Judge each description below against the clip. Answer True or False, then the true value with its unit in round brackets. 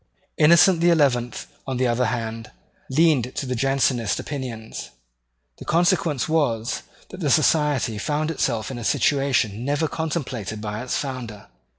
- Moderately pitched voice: False (130 Hz)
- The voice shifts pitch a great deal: False (4.8 semitones)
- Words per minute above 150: False (145 wpm)